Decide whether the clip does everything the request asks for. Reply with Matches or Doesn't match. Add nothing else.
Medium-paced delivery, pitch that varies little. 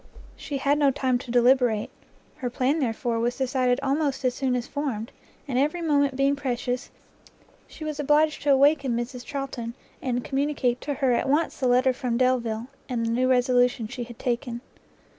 Matches